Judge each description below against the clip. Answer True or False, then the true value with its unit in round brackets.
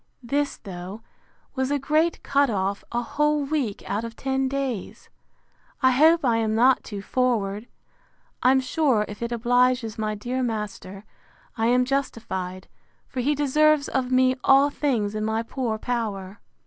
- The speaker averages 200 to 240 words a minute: False (155 wpm)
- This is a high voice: True (245 Hz)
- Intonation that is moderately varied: True (4.0 semitones)